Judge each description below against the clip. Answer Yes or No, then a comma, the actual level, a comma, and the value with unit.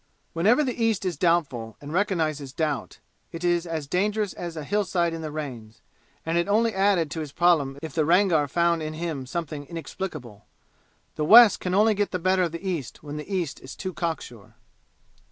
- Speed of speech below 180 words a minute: No, average, 195 wpm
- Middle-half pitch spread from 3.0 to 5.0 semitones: Yes, average, 3.9 semitones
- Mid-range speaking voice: Yes, medium, 170 Hz